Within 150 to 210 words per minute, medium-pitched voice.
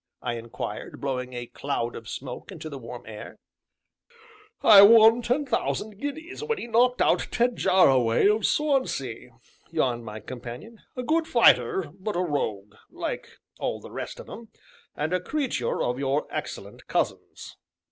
Yes: average, 155 wpm; medium, 160 Hz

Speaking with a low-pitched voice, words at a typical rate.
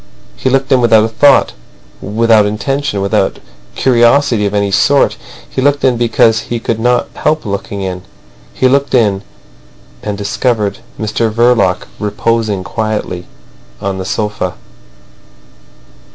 No: low, 110 Hz; slow, 130 wpm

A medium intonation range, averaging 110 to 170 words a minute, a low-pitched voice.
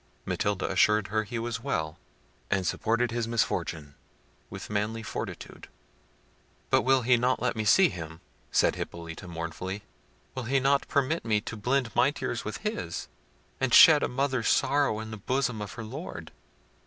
Yes: average, 4.3 semitones; average, 165 wpm; low, 115 Hz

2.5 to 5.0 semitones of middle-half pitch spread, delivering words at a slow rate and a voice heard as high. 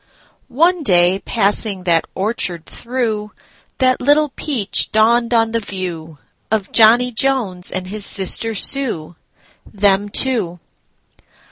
Yes: average, 4.5 semitones; slow, 100 wpm; high, 215 Hz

